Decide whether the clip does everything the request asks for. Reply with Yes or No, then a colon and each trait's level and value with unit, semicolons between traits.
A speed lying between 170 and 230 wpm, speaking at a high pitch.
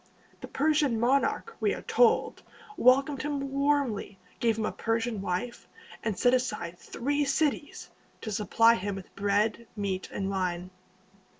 No: average, 140 wpm; high, 230 Hz